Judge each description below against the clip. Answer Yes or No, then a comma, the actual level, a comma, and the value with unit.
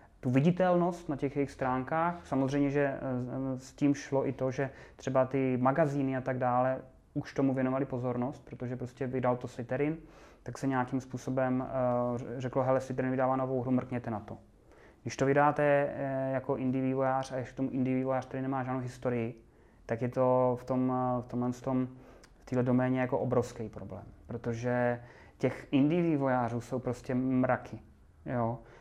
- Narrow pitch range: Yes, narrow, 1.3 semitones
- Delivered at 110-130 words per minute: No, average, 165 wpm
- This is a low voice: Yes, low, 130 Hz